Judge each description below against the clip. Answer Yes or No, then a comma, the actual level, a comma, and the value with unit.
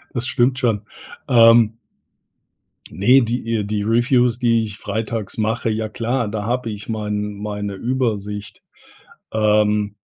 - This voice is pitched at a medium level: No, low, 110 Hz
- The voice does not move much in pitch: Yes, narrow, 2.3 semitones